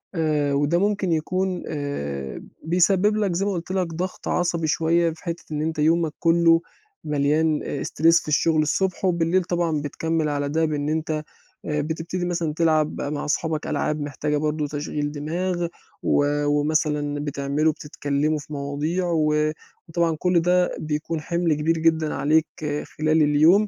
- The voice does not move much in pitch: Yes, narrow, 2.3 semitones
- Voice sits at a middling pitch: Yes, medium, 155 Hz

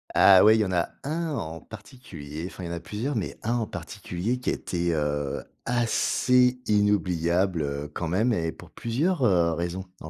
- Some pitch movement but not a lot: No, wide, 5.9 semitones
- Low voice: Yes, very low, 95 Hz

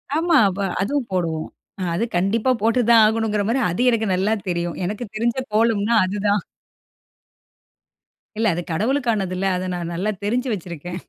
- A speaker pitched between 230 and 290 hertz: No, high, 210 Hz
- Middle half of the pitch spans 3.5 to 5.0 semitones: Yes, average, 4.1 semitones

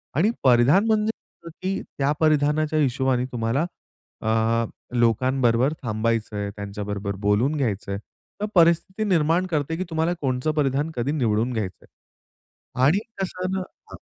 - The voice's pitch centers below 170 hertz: Yes, low, 135 Hz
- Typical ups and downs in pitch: No, wide, 5.9 semitones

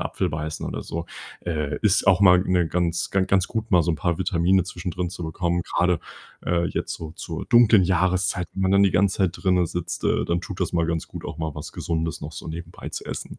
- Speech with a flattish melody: Yes, narrow, 2.1 semitones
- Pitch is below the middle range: Yes, very low, 90 Hz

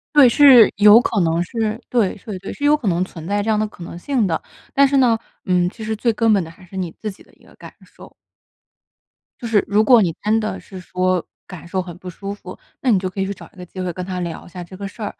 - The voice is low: No, high, 200 Hz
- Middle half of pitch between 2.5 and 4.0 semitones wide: Yes, average, 3.6 semitones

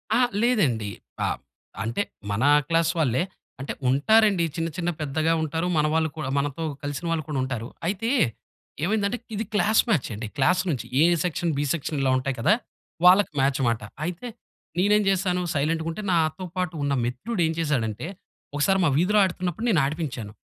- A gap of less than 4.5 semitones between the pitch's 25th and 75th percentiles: No, average, 5.0 semitones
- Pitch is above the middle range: No, medium, 160 Hz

